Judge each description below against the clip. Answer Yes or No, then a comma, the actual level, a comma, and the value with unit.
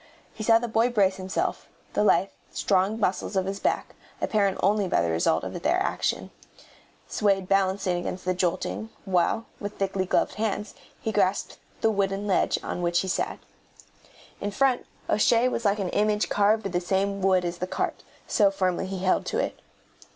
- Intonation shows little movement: Yes, narrow, 2.2 semitones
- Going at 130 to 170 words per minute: No, average, 180 wpm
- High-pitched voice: Yes, high, 195 Hz